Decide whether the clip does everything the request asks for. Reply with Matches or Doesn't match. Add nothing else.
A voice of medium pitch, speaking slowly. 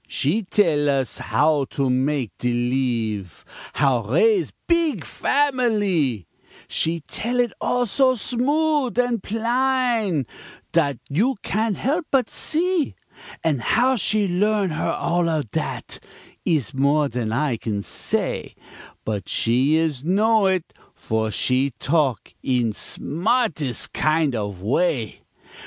Matches